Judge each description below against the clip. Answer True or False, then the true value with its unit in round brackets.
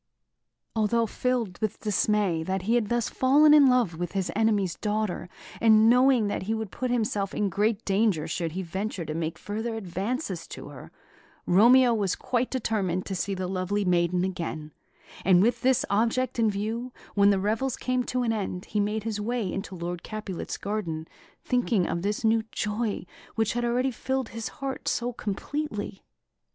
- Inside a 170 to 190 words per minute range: True (175 wpm)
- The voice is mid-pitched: False (210 Hz)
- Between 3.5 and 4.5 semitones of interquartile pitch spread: True (3.8 semitones)